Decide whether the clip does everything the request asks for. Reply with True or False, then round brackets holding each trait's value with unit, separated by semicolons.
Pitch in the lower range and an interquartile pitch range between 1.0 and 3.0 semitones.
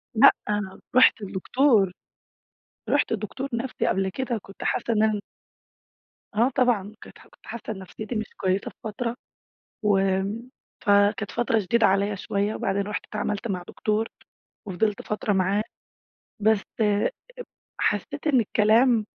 False (210 Hz; 2.7 semitones)